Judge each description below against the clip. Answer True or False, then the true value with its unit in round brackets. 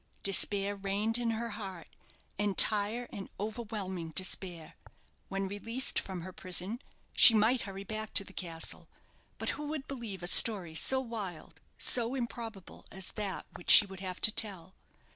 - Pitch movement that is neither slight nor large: True (3.3 semitones)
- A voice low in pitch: False (205 Hz)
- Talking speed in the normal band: True (155 wpm)